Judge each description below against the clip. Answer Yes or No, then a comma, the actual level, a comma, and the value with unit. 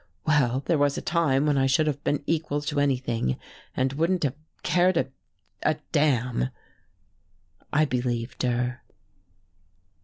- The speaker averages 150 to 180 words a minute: No, slow, 135 wpm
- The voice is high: No, medium, 140 Hz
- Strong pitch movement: No, average, 3.3 semitones